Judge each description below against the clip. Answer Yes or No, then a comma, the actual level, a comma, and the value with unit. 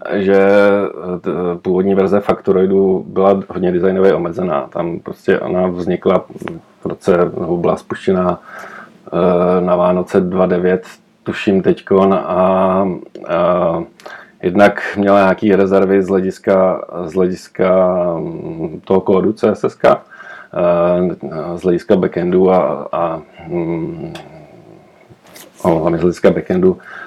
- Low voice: Yes, very low, 95 Hz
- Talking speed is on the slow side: Yes, slow, 100 wpm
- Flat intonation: Yes, narrow, 1.7 semitones